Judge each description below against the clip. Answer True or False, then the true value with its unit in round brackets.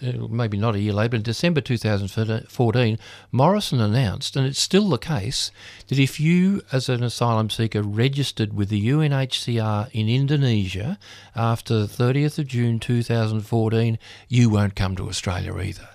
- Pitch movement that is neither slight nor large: True (3.7 semitones)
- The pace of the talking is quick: False (155 wpm)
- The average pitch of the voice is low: True (115 Hz)